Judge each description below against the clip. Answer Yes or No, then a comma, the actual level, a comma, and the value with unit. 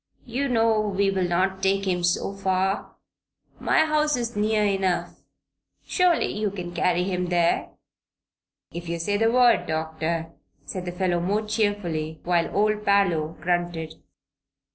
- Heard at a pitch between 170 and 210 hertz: Yes, high, 190 Hz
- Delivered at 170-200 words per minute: No, average, 140 wpm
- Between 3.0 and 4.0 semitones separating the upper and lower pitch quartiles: Yes, average, 3.4 semitones